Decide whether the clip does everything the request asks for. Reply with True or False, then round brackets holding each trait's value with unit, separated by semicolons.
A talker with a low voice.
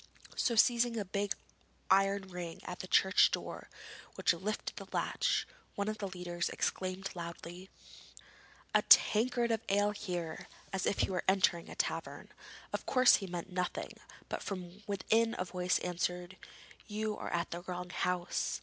False (190 Hz)